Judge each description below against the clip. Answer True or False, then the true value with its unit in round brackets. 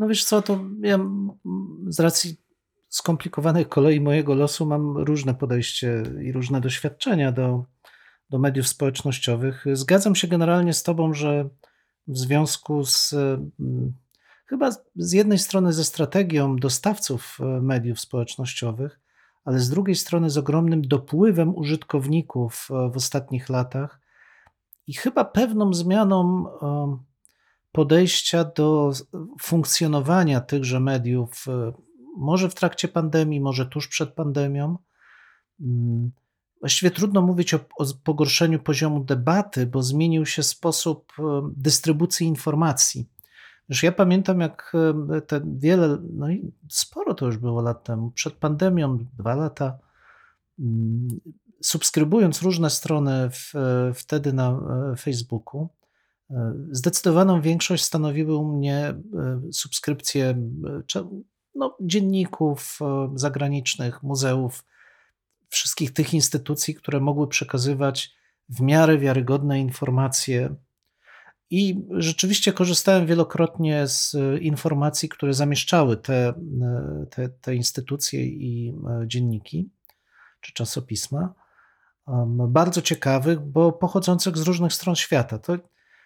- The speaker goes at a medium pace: False (105 wpm)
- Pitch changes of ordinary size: True (4.3 semitones)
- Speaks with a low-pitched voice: False (150 Hz)